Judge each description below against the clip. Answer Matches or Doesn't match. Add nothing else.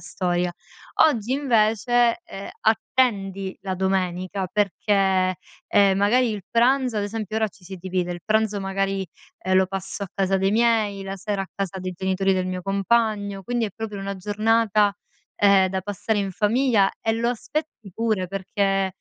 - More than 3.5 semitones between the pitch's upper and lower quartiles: Doesn't match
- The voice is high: Matches